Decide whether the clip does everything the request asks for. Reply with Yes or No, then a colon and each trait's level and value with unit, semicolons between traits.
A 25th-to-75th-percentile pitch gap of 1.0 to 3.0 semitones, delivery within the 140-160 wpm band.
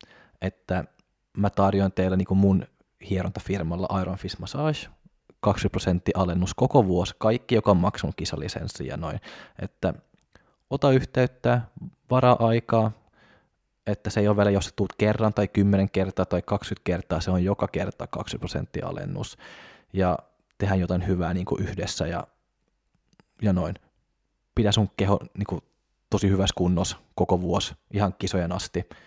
Yes: narrow, 2.5 semitones; average, 145 wpm